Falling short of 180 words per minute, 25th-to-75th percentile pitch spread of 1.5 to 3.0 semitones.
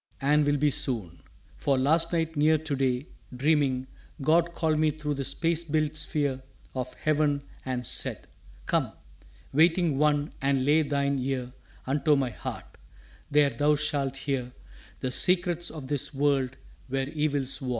Yes: average, 155 wpm; narrow, 2.4 semitones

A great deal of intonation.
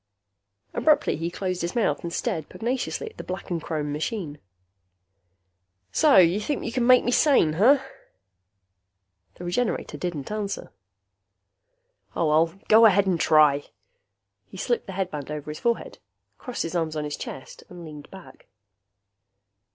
Yes: wide, 6.5 semitones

